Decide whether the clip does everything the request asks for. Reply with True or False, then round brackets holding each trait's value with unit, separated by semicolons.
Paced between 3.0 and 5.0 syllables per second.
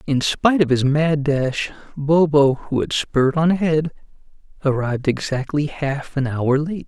True (4.5 syllables/s)